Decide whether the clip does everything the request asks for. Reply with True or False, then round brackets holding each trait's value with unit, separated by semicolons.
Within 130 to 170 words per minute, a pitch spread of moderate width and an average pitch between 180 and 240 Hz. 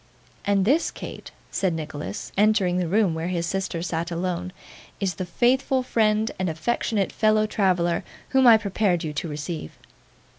True (155 wpm; 4.1 semitones; 185 Hz)